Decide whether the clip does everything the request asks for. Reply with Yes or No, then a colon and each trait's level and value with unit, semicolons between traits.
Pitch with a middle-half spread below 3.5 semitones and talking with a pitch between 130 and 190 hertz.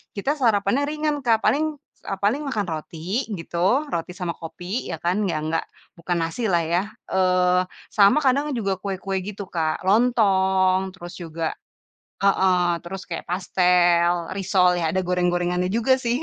Yes: narrow, 2.6 semitones; medium, 185 Hz